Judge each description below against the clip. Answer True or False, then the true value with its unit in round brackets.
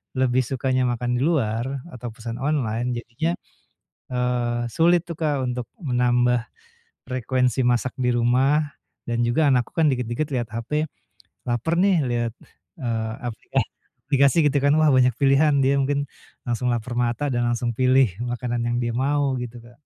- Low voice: True (125 Hz)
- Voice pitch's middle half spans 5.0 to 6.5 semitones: False (2.7 semitones)